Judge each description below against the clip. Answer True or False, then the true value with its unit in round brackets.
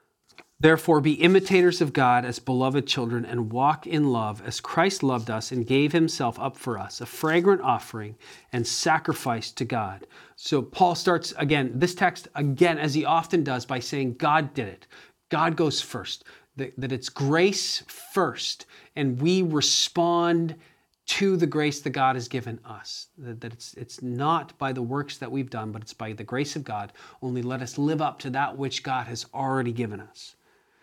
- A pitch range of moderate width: True (4.7 semitones)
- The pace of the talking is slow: False (180 wpm)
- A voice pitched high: False (135 Hz)